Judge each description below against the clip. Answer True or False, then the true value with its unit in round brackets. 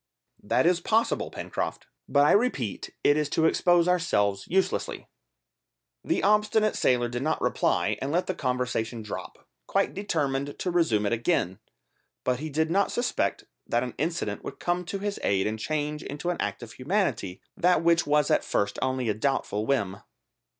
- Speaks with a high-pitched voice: False (145 Hz)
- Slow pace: False (170 wpm)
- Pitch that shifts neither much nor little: False (6.7 semitones)